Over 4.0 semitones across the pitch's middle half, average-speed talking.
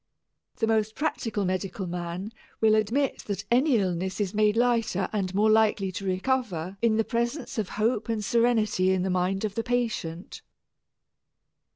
No: average, 3.5 semitones; average, 160 wpm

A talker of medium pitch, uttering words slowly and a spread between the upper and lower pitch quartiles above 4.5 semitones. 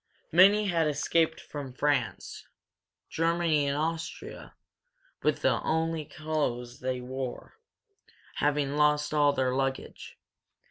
No: medium, 150 Hz; slow, 105 wpm; average, 3.3 semitones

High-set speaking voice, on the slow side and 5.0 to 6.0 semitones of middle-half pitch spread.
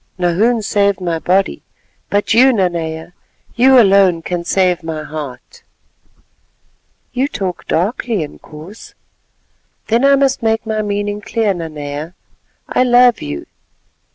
Yes: high, 195 Hz; slow, 120 wpm; average, 5.3 semitones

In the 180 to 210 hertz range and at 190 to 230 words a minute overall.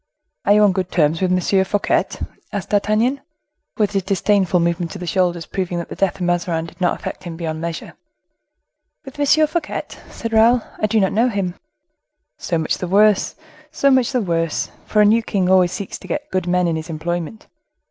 Yes: high, 190 Hz; average, 200 wpm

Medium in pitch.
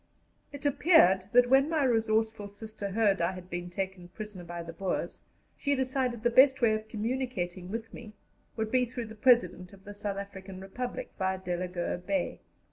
No: high, 215 Hz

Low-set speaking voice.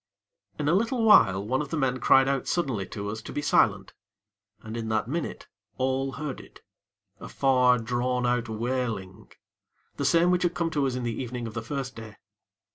Yes: low, 130 Hz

